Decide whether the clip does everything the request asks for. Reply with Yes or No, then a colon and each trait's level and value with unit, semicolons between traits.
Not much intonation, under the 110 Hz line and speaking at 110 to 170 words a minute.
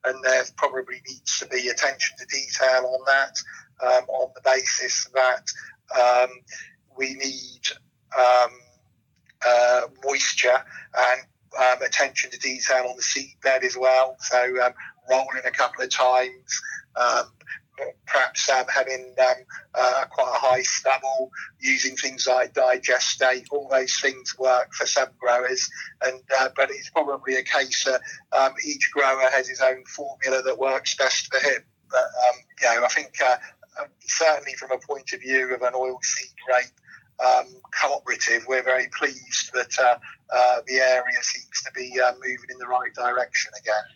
No: narrow, 0.8 semitones; low, 130 Hz; average, 160 wpm